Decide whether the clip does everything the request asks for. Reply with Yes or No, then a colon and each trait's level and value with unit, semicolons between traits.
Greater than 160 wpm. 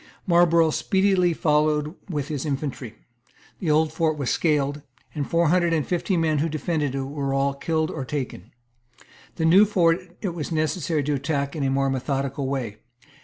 Yes: average, 170 wpm